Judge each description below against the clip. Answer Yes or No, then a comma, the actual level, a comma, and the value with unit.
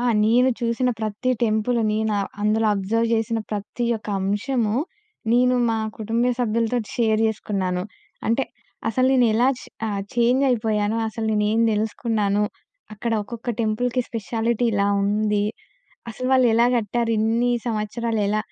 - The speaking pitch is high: Yes, high, 225 Hz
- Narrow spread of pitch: Yes, narrow, 2.0 semitones